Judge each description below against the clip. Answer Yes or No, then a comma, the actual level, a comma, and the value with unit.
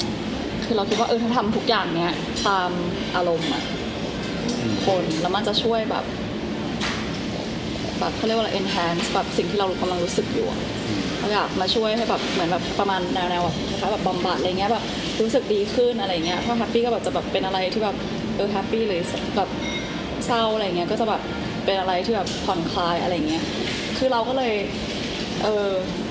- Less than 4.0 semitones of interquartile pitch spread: Yes, average, 3.6 semitones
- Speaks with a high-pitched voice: Yes, high, 205 Hz